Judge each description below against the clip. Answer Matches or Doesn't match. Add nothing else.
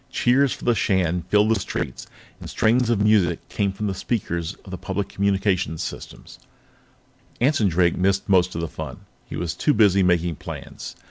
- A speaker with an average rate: Matches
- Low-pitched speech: Matches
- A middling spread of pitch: Matches